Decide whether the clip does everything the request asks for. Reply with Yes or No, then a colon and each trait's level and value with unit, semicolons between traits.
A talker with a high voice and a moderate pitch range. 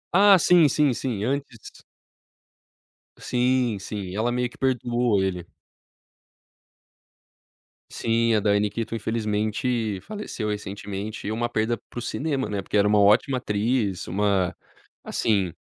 No: low, 110 Hz; average, 3.3 semitones